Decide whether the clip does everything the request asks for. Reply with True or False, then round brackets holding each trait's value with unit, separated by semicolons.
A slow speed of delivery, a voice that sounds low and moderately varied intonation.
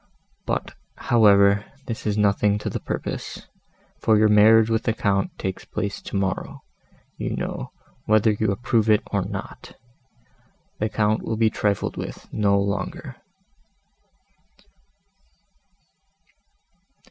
False (110 wpm; 105 Hz; 1.6 semitones)